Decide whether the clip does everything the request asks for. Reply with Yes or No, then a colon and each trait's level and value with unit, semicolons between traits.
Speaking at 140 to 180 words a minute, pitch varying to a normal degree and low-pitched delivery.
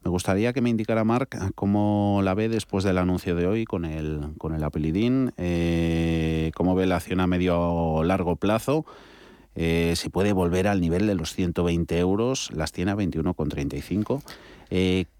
Yes: average, 175 wpm; average, 3.5 semitones; very low, 90 Hz